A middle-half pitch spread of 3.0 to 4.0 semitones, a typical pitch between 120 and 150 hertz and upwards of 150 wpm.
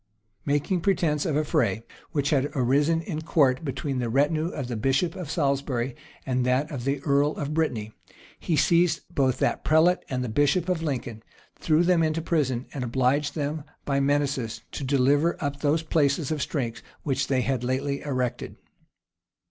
Yes: average, 3.3 semitones; medium, 140 Hz; average, 175 wpm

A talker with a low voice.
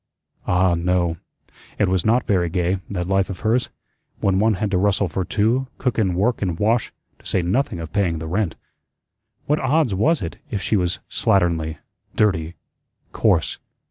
Yes: very low, 95 Hz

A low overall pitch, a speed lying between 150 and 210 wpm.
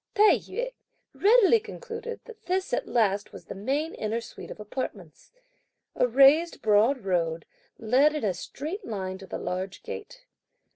No: very high, 265 Hz; average, 155 wpm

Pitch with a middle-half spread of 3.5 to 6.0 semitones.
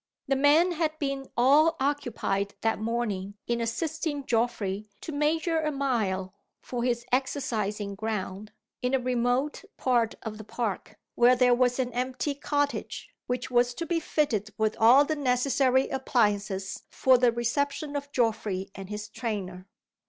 Yes: average, 4.5 semitones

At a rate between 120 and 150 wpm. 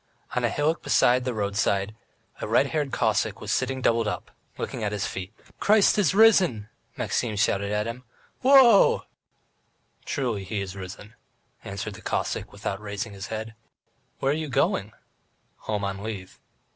No: average, 165 wpm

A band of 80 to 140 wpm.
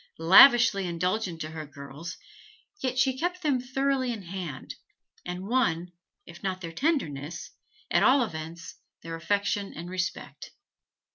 Yes: slow, 135 wpm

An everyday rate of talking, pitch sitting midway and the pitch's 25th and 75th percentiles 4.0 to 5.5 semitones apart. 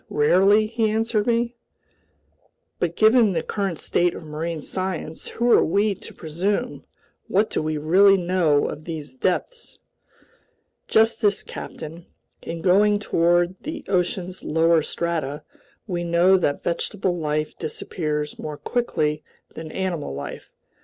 No: slow, 130 wpm; medium, 175 Hz; average, 4.6 semitones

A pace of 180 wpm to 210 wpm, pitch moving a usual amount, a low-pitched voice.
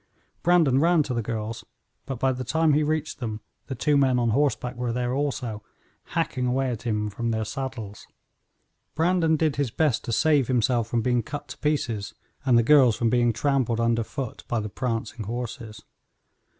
Yes: average, 185 wpm; average, 3.6 semitones; low, 125 Hz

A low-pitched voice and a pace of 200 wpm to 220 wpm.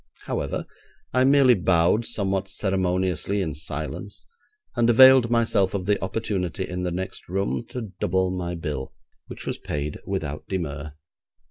No: very low, 95 Hz; average, 140 wpm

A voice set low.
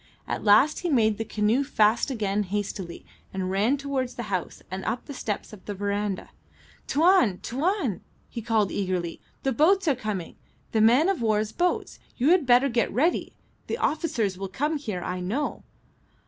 No: high, 225 Hz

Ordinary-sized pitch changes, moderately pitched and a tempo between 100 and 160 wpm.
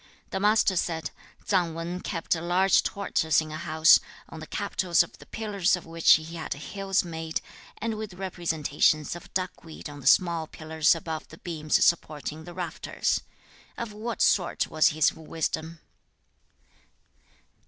Yes: average, 3.0 semitones; medium, 165 Hz; average, 155 wpm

